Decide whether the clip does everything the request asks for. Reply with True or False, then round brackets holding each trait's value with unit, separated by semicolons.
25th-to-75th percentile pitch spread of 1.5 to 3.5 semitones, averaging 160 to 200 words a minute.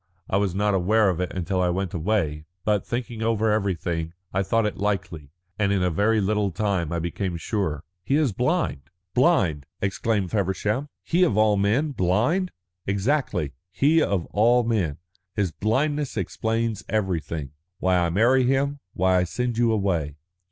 False (4.2 semitones; 170 wpm)